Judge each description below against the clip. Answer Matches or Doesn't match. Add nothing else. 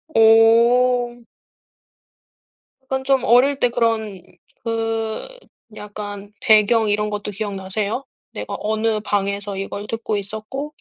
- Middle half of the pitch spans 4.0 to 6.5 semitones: Doesn't match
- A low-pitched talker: Doesn't match